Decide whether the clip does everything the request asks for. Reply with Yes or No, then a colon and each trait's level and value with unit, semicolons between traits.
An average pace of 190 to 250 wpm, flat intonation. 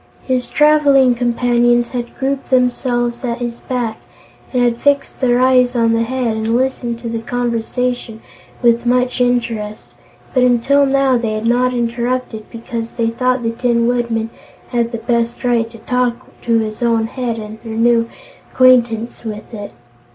No: average, 160 wpm; narrow, 1.6 semitones